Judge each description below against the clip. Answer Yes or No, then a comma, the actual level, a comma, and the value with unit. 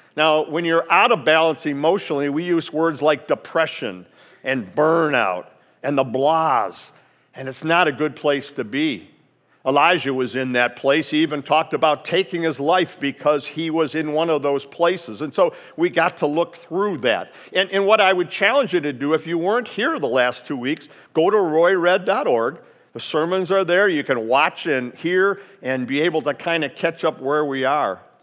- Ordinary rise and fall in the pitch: Yes, average, 3.5 semitones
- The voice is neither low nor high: Yes, medium, 160 Hz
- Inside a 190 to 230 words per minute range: Yes, average, 200 wpm